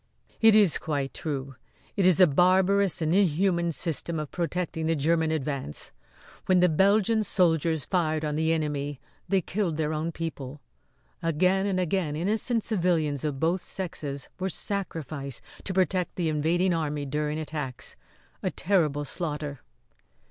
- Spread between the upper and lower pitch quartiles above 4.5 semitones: No, average, 3.7 semitones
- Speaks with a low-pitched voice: No, medium, 165 Hz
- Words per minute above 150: No, average, 145 wpm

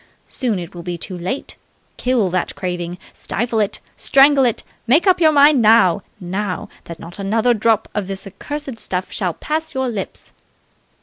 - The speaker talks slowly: No, average, 170 wpm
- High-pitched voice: Yes, high, 215 Hz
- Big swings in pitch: Yes, wide, 6.3 semitones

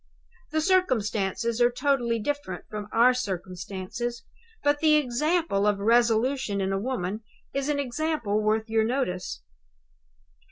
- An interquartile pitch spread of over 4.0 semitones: Yes, average, 5.2 semitones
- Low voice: No, high, 235 Hz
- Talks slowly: Yes, slow, 125 wpm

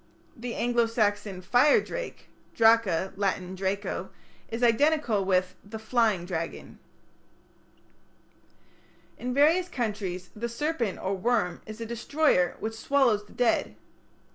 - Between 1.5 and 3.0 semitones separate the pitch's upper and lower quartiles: No, average, 4.1 semitones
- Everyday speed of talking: No, slow, 115 wpm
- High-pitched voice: Yes, high, 225 Hz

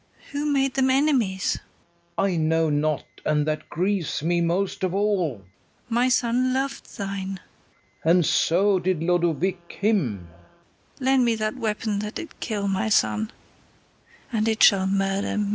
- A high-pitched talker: Yes, high, 195 Hz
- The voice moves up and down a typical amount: Yes, average, 4.6 semitones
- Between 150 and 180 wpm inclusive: Yes, average, 160 wpm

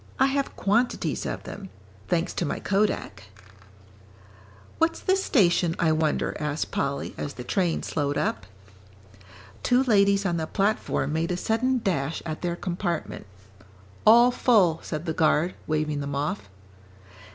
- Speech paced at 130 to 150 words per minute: Yes, average, 140 wpm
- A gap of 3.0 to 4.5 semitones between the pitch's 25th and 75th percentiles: No, wide, 5.4 semitones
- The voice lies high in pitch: No, medium, 175 Hz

